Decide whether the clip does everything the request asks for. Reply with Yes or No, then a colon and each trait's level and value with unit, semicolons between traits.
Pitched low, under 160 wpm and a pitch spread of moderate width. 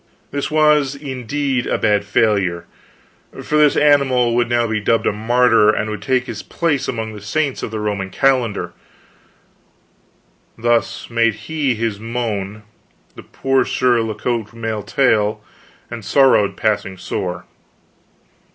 Yes: low, 115 Hz; average, 140 wpm; average, 3.8 semitones